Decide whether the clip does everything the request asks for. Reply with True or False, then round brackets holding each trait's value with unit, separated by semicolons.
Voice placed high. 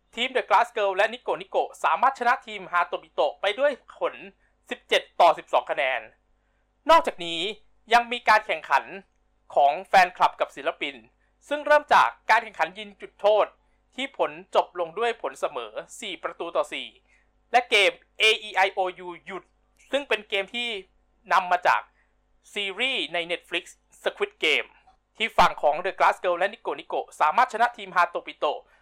True (220 Hz)